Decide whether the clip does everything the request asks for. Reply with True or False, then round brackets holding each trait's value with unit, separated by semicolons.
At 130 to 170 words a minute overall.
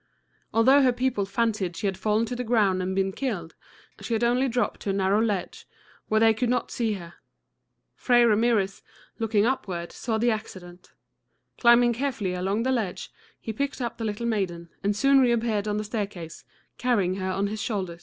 False (185 wpm)